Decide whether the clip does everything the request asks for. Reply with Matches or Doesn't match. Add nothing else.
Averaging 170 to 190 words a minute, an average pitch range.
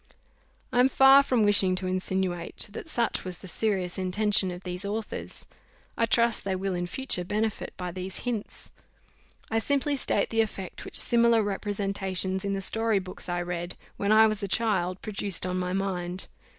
Matches